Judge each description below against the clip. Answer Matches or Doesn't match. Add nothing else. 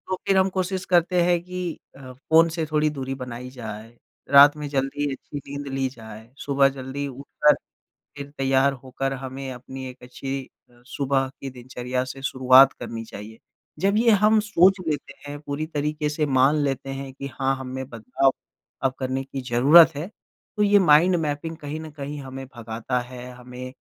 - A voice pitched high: Doesn't match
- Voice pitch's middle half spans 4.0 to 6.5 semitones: Doesn't match